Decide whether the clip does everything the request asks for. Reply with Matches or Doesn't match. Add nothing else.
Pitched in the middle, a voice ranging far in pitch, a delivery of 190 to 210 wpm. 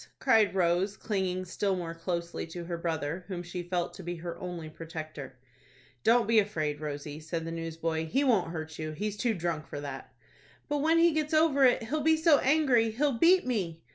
Matches